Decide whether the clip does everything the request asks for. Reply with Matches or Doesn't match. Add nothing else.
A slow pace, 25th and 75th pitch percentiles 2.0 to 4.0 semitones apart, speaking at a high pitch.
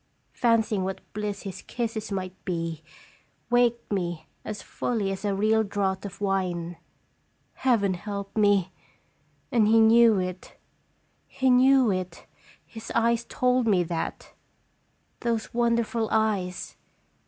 Matches